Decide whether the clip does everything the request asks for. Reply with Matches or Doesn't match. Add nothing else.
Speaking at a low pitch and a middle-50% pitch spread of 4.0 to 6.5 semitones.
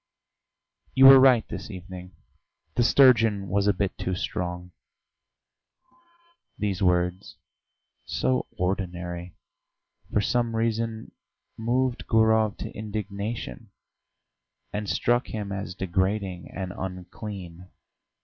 Doesn't match